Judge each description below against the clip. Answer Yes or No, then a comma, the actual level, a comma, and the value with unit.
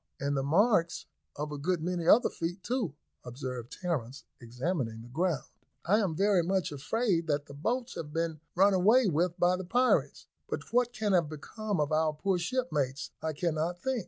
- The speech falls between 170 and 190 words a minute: Yes, average, 185 wpm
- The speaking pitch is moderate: Yes, medium, 170 Hz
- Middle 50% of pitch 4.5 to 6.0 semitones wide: Yes, average, 4.9 semitones